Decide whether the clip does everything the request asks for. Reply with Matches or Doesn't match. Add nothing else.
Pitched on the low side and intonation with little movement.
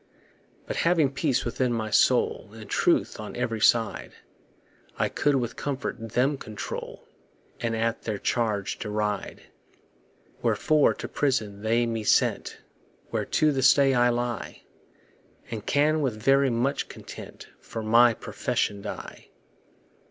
Doesn't match